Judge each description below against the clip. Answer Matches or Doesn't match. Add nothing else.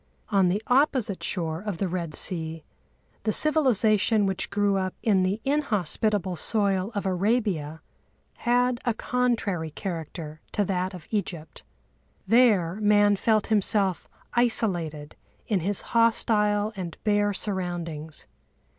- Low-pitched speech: Doesn't match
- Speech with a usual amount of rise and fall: Matches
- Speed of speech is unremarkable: Doesn't match